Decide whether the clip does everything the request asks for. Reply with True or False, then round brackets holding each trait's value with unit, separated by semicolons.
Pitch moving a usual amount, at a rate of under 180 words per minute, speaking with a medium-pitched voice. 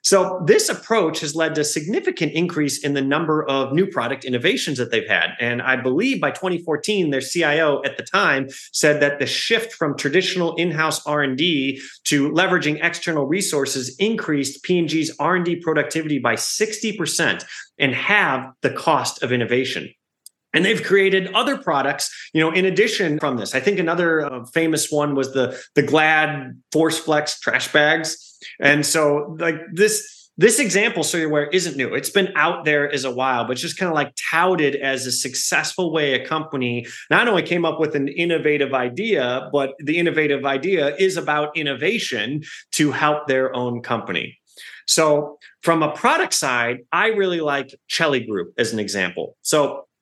True (3.6 semitones; 170 wpm; 150 Hz)